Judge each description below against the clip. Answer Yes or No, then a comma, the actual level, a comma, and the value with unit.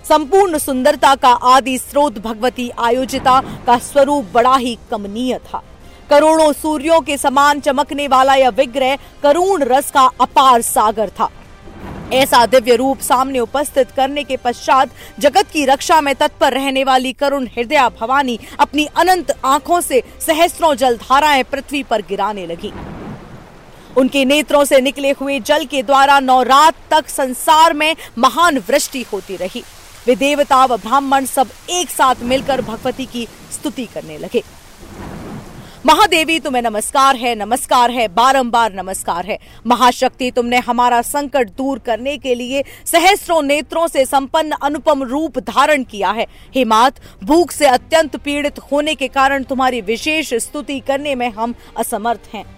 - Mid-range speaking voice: No, very high, 270 Hz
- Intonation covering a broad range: No, average, 2.9 semitones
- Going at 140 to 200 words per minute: Yes, average, 145 wpm